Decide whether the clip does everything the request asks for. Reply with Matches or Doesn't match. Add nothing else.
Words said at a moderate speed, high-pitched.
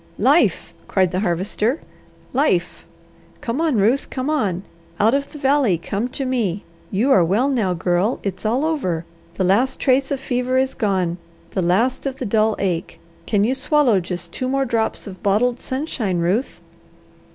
Matches